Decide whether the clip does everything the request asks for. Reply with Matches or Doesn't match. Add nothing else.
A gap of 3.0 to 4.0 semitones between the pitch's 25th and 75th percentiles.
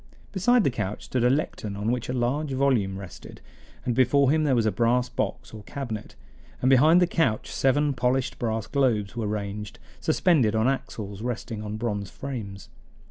Doesn't match